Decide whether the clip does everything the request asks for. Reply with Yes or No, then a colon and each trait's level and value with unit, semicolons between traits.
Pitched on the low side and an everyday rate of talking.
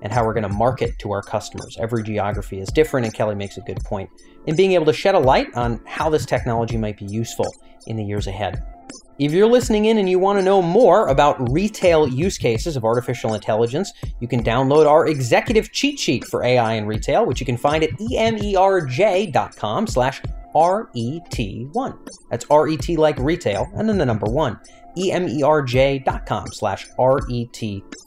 Yes: low, 130 Hz; average, 180 wpm